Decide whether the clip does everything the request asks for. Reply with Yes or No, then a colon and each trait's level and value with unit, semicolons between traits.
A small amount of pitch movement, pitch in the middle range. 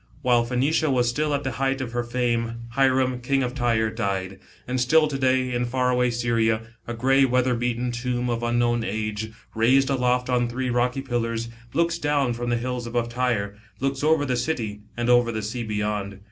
No: narrow, 1.8 semitones; low, 120 Hz